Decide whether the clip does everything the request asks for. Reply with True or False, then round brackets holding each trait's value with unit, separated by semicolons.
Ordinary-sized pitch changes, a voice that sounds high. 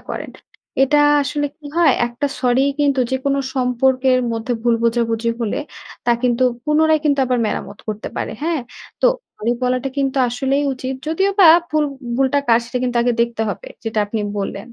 True (3.4 semitones; 255 Hz)